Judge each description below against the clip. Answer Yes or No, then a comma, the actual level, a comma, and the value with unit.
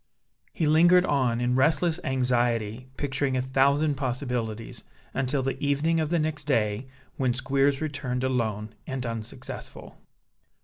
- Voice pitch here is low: Yes, low, 130 Hz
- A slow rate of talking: Yes, slow, 130 wpm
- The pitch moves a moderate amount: Yes, average, 3.0 semitones